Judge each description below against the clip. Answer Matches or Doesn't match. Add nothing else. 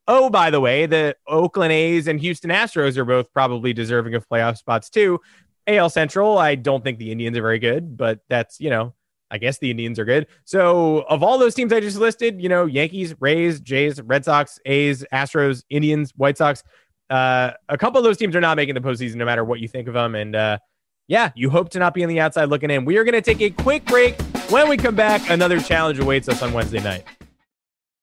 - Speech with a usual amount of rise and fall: Doesn't match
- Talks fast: Matches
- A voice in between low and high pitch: Matches